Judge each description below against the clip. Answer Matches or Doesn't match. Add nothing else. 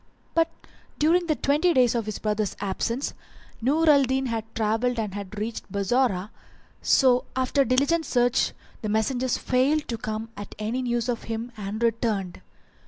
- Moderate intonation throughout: Matches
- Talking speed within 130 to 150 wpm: Doesn't match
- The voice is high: Matches